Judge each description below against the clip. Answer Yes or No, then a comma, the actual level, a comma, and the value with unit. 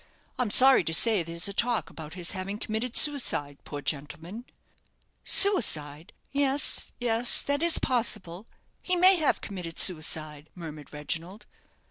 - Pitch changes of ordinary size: No, wide, 7.4 semitones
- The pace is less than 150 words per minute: Yes, slow, 135 wpm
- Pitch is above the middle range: Yes, high, 195 Hz